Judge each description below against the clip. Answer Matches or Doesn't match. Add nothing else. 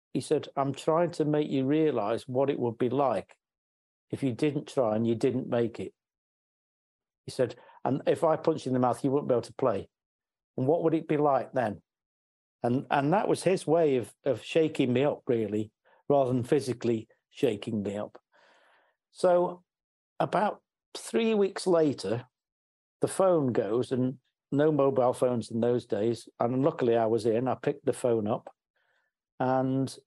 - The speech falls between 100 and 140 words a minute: Doesn't match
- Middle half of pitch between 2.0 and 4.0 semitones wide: Doesn't match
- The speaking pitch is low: Matches